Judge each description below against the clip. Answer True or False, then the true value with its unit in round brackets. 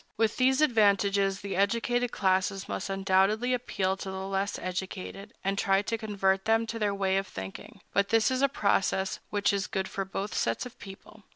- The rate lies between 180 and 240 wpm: True (190 wpm)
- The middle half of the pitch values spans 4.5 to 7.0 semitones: False (2.5 semitones)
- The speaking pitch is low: False (200 Hz)